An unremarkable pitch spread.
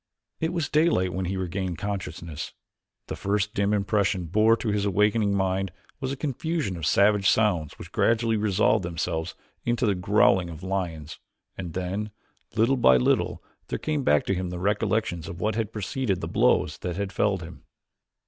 Yes: average, 3.4 semitones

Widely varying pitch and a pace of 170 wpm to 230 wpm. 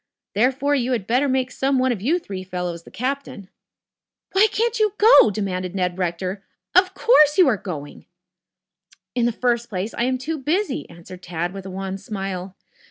Yes: wide, 6.9 semitones; average, 180 wpm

